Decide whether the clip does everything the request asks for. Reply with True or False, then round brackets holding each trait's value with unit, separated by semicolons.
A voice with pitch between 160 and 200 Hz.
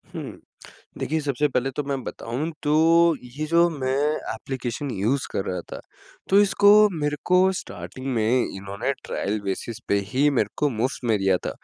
False (135 Hz)